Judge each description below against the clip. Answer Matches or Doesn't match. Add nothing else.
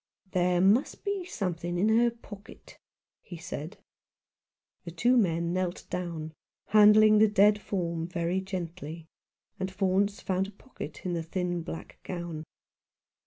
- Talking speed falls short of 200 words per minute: Matches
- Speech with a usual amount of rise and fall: Matches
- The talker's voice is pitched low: Doesn't match